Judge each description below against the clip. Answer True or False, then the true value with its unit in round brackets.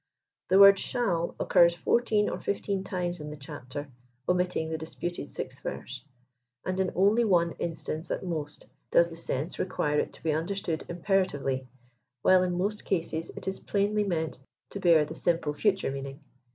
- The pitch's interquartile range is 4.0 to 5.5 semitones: False (3.4 semitones)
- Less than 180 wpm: True (165 wpm)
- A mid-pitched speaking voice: True (175 Hz)